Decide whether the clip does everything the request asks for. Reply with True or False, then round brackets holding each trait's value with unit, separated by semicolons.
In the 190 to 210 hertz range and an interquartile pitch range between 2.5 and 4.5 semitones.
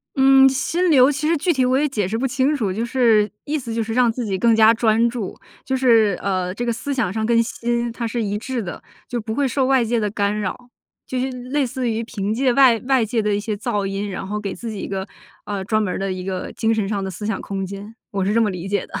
False (225 Hz; 3.8 semitones)